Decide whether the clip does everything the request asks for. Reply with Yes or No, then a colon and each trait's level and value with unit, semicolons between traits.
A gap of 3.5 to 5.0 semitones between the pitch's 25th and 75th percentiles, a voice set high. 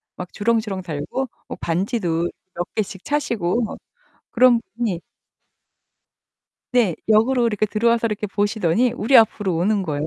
Yes: average, 4.4 semitones; high, 210 Hz